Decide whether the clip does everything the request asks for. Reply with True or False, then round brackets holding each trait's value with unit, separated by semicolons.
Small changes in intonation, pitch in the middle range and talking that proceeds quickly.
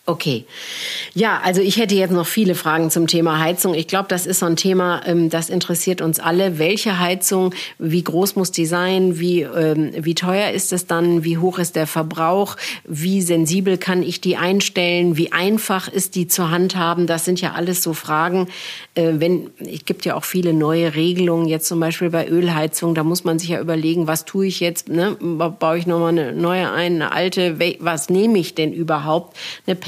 True (1.9 semitones; 175 Hz; 200 wpm)